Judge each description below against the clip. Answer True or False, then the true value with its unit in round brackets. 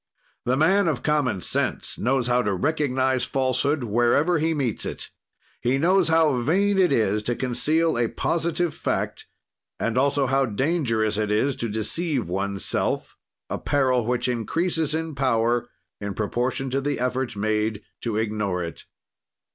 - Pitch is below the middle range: True (130 Hz)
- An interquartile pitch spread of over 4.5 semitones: True (5.1 semitones)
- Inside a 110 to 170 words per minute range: True (150 wpm)